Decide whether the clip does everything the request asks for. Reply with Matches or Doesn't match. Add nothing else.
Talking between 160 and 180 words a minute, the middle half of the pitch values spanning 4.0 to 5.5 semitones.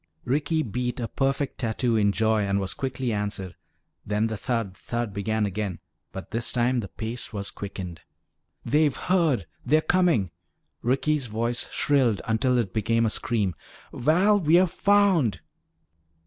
Doesn't match